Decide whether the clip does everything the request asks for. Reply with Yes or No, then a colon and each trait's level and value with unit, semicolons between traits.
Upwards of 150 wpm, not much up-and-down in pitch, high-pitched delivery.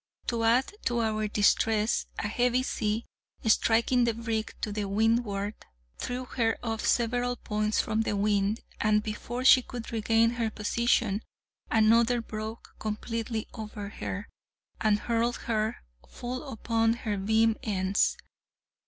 No: slow, 135 wpm; narrow, 1.8 semitones; high, 225 Hz